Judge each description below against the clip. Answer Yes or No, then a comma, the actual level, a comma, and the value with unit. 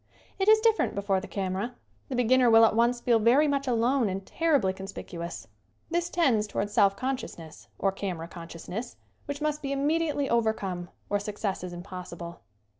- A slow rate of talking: No, average, 170 wpm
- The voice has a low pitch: No, high, 225 Hz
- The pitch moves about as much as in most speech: No, wide, 6.2 semitones